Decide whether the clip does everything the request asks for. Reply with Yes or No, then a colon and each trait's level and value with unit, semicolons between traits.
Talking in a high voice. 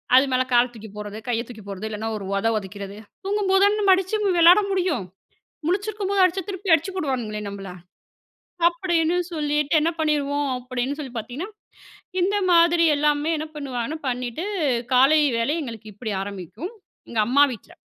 Yes: very high, 290 Hz